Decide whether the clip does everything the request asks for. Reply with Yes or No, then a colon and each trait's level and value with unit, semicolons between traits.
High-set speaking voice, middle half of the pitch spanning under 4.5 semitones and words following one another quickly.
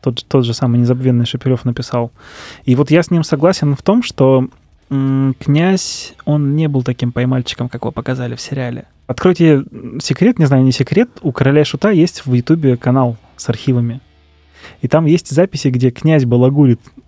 No: low, 130 Hz; average, 3.6 semitones; fast, 180 wpm